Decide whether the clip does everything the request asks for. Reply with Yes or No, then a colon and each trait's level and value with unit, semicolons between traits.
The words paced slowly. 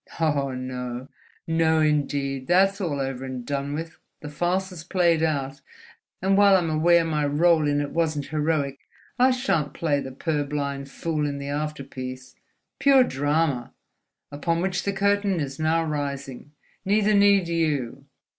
No: average, 145 wpm